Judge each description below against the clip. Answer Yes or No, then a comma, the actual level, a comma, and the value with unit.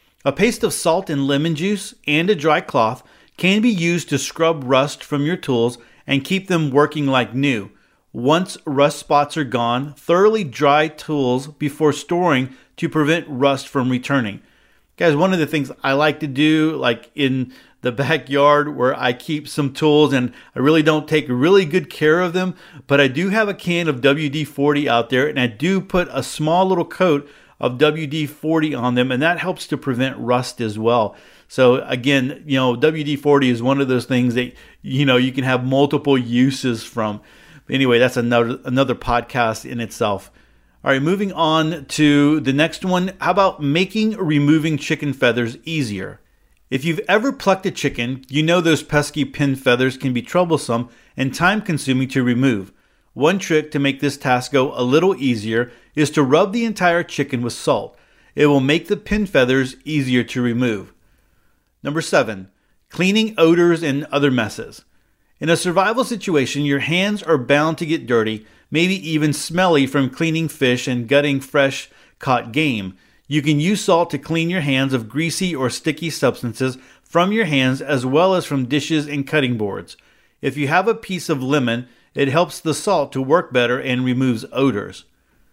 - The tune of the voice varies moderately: Yes, average, 4.1 semitones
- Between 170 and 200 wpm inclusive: Yes, average, 180 wpm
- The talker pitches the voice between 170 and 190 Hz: No, medium, 145 Hz